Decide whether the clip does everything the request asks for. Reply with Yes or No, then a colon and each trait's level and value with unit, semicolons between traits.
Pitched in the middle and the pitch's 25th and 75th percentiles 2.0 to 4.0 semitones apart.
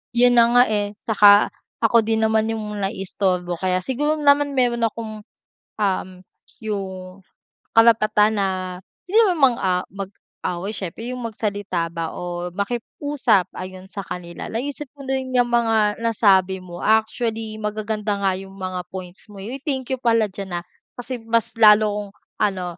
No: high, 215 Hz; average, 3.6 semitones